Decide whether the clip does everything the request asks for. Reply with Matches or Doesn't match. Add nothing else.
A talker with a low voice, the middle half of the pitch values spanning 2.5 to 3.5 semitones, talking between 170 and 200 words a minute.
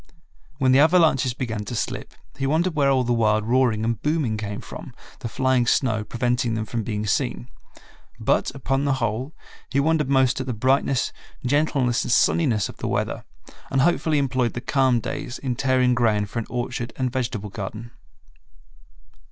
Matches